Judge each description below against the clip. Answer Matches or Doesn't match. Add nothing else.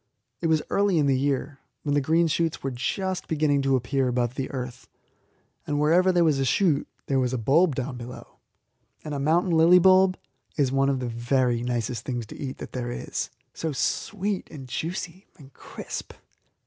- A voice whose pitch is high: Doesn't match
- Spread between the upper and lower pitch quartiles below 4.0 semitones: Doesn't match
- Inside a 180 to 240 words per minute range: Matches